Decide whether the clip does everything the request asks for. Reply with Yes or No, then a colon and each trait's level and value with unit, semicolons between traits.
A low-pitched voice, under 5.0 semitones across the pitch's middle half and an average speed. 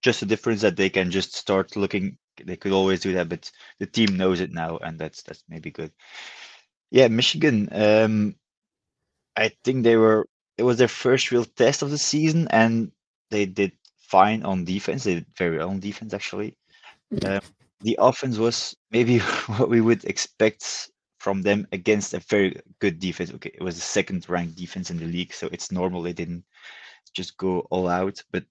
Yes: low, 100 Hz; average, 3.8 semitones; average, 190 wpm